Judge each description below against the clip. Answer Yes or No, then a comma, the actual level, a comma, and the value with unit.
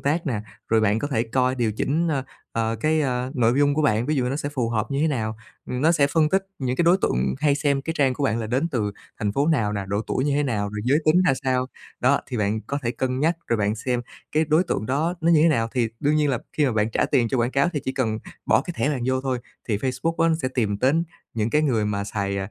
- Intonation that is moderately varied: Yes, average, 4.8 semitones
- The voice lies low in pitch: Yes, low, 130 Hz